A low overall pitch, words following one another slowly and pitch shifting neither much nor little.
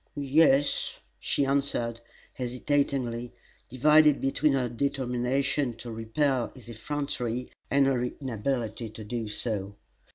Yes: low, 125 Hz; slow, 110 wpm; average, 3.0 semitones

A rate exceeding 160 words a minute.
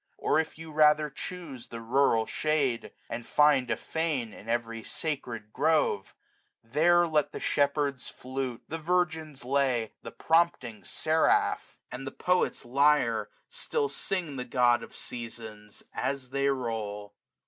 No: average, 140 wpm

